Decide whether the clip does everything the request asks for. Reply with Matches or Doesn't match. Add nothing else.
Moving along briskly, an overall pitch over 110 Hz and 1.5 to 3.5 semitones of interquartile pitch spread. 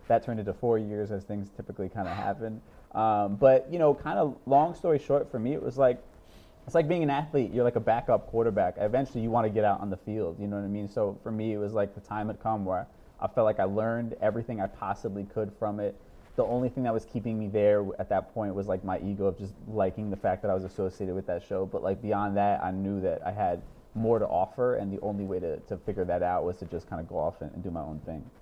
Doesn't match